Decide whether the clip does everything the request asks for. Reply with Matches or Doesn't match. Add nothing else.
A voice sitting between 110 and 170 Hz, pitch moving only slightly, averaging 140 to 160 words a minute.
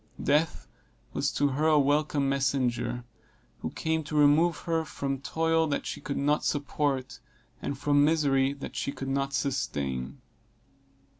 Matches